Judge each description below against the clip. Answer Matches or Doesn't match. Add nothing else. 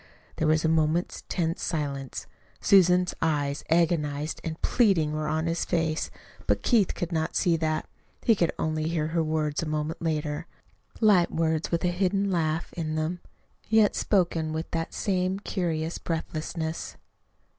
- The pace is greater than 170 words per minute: Doesn't match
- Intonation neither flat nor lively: Doesn't match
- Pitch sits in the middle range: Matches